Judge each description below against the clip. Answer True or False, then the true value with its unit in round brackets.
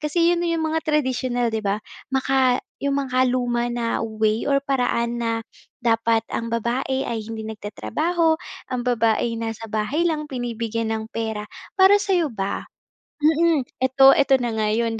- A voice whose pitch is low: False (245 Hz)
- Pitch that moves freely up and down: False (3.9 semitones)